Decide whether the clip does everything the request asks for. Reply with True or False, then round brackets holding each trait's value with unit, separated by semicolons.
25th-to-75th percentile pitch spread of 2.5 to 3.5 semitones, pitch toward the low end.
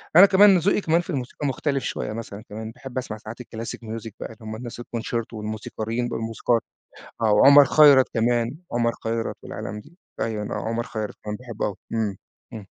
True (3.1 semitones; 115 Hz)